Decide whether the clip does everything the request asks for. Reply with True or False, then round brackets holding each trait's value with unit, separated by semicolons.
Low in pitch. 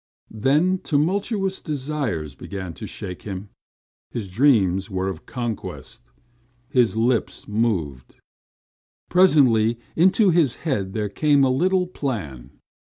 True (120 Hz)